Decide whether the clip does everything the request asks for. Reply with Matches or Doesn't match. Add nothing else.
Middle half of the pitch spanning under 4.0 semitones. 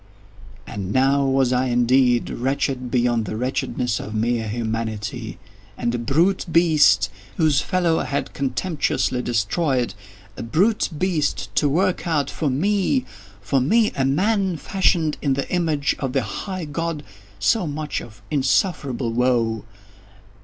Doesn't match